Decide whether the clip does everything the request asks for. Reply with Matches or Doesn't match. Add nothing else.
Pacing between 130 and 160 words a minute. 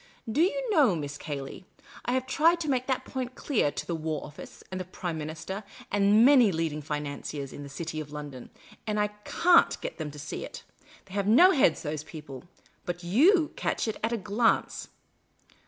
Doesn't match